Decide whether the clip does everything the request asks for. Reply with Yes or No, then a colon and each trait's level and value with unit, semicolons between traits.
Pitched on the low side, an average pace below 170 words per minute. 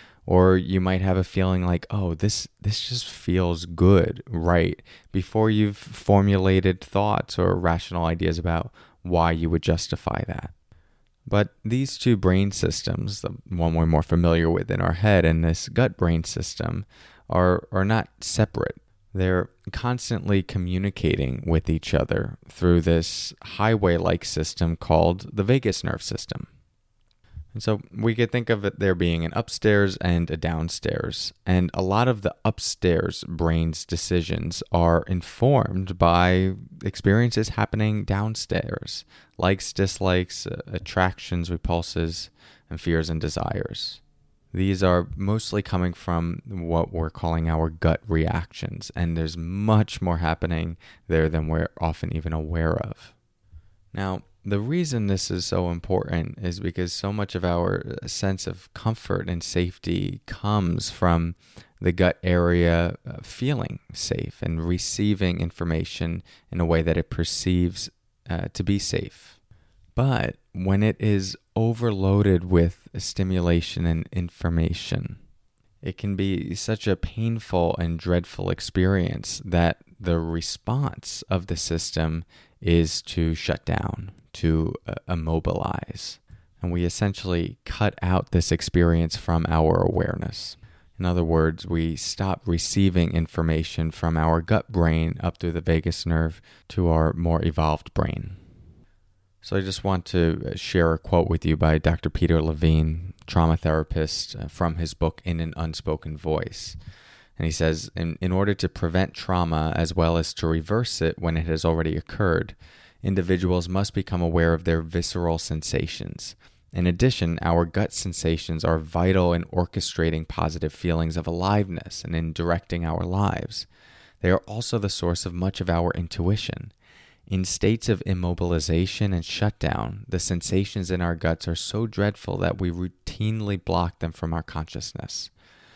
Yes: very low, 90 Hz; average, 145 wpm